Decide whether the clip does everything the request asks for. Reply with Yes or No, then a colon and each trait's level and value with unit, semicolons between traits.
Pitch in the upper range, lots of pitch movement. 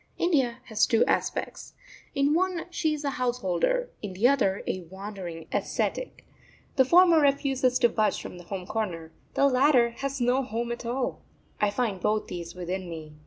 Yes: high, 240 Hz; wide, 6.5 semitones